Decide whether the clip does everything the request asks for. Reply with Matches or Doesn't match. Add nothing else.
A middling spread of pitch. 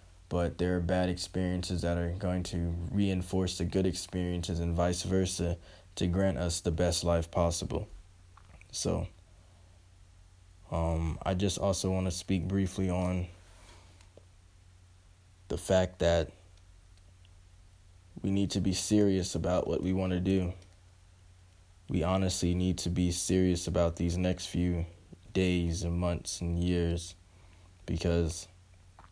Doesn't match